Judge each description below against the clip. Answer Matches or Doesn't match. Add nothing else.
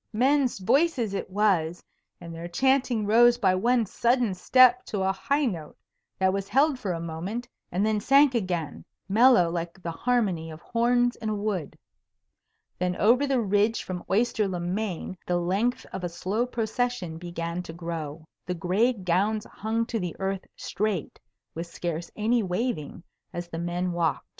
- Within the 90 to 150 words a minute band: Doesn't match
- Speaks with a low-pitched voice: Doesn't match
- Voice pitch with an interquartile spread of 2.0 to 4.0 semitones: Doesn't match